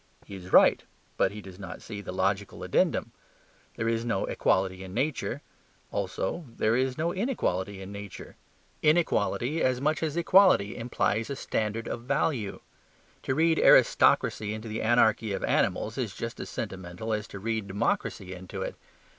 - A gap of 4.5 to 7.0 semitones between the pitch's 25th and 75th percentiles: Yes, average, 5.2 semitones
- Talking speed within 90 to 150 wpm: No, average, 165 wpm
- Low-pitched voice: Yes, low, 110 Hz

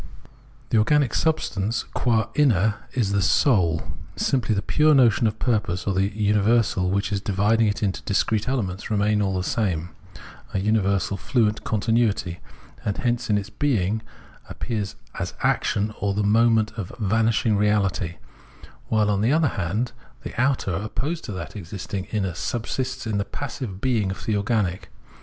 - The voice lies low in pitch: Yes, low, 105 Hz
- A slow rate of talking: No, average, 155 wpm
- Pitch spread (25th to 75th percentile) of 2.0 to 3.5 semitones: Yes, average, 2.8 semitones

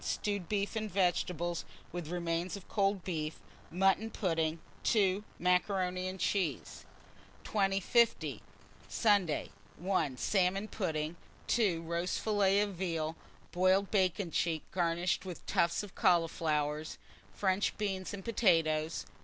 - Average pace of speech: No, slow, 115 wpm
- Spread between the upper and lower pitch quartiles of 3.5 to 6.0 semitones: No, average, 3.0 semitones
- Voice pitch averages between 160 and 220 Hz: Yes, medium, 185 Hz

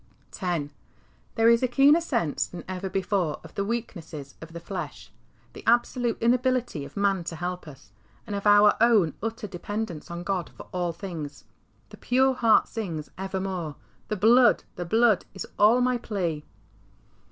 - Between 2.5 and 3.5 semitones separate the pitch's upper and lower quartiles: No, average, 5.2 semitones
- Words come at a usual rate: Yes, average, 165 wpm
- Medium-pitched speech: No, high, 195 Hz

